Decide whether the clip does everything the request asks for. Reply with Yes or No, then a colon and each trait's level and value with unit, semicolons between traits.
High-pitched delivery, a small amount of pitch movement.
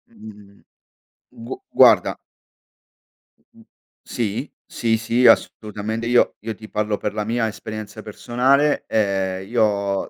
No: low, 110 Hz; narrow, 2.2 semitones